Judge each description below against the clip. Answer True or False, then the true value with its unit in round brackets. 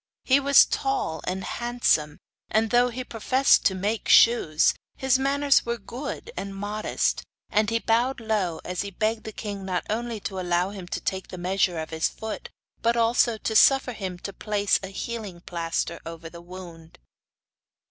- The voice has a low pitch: False (210 Hz)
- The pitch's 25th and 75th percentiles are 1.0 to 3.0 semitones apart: False (4.5 semitones)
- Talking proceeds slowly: False (175 wpm)